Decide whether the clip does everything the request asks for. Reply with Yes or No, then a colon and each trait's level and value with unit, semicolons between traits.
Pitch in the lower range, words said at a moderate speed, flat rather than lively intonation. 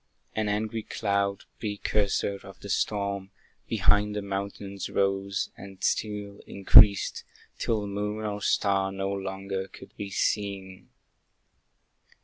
No: low, 100 Hz; slow, 115 wpm; narrow, 1.1 semitones